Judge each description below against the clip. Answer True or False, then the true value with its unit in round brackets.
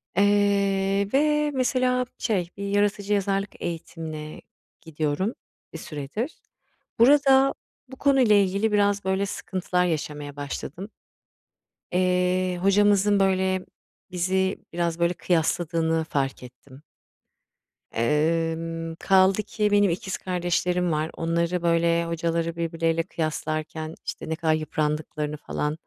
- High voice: False (180 Hz)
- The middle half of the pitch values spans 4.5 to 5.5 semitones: False (3.7 semitones)